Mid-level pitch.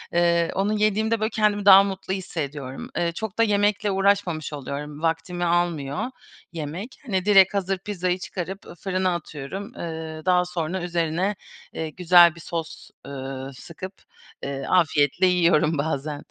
Yes: medium, 175 Hz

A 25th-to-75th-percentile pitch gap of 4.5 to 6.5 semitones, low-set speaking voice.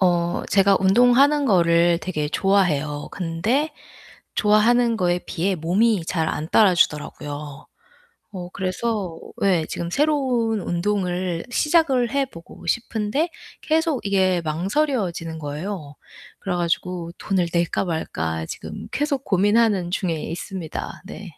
No: average, 5.2 semitones; medium, 185 Hz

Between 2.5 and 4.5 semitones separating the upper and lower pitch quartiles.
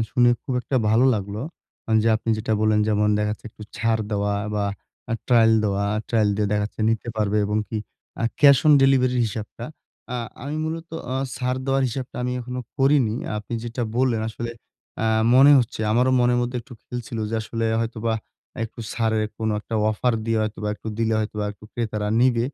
Yes: average, 2.8 semitones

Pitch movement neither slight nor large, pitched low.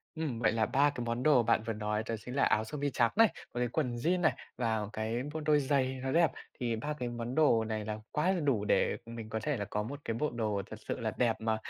Yes: average, 4.5 semitones; low, 120 Hz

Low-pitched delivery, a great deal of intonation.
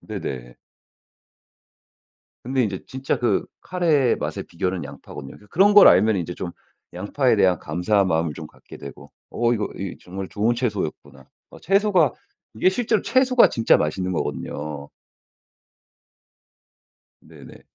Yes: low, 105 Hz; wide, 7.5 semitones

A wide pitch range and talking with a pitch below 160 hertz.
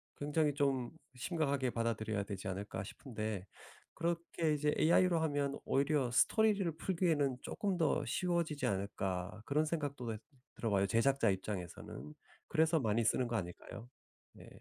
Yes: wide, 6.4 semitones; low, 135 Hz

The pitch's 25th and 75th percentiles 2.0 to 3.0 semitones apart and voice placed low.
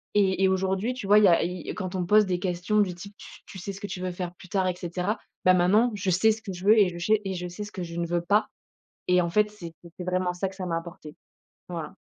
No: narrow, 2.4 semitones; medium, 185 Hz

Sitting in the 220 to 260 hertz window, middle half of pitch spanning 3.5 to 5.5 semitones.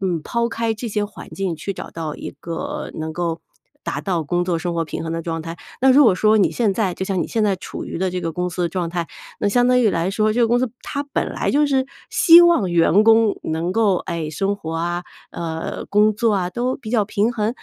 No: high, 195 Hz; average, 5.0 semitones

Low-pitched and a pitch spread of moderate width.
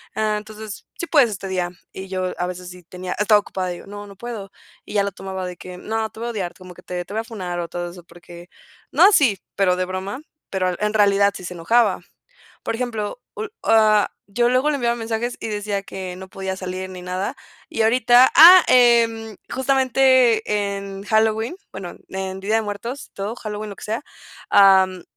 No: high, 205 Hz; average, 3.3 semitones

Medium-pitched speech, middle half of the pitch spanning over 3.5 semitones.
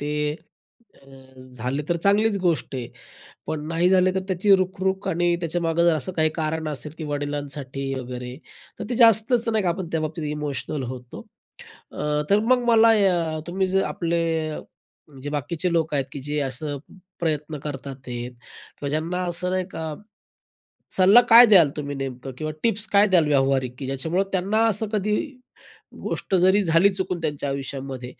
Yes: medium, 160 Hz; average, 4.8 semitones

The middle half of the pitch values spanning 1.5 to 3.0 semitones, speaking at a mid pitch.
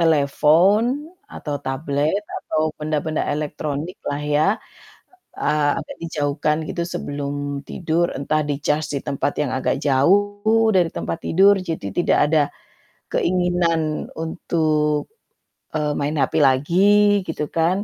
No: average, 3.4 semitones; medium, 155 Hz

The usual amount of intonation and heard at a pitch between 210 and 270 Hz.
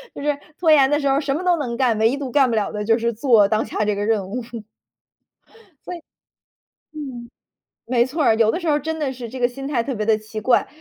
Yes: average, 4.2 semitones; high, 245 Hz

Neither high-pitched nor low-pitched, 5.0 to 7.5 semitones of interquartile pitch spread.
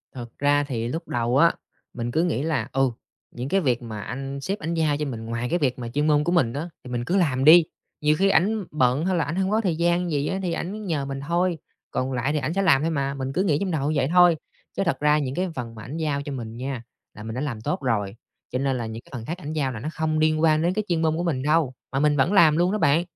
No: medium, 150 Hz; average, 4.6 semitones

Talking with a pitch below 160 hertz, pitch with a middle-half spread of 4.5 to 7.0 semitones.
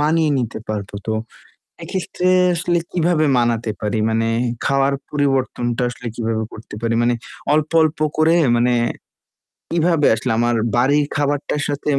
Yes: low, 135 Hz; average, 4.9 semitones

